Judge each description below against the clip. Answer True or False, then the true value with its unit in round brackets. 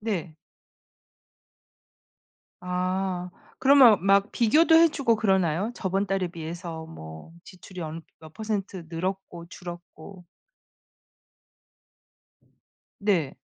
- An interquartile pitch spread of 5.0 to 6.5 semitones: False (3.3 semitones)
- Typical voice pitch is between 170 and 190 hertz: True (185 Hz)